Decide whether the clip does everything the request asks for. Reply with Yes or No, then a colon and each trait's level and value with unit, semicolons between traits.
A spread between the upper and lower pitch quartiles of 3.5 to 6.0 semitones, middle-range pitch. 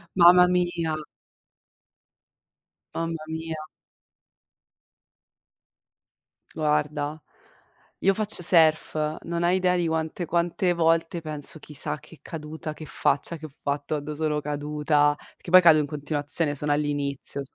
No: narrow, 2.4 semitones; medium, 155 Hz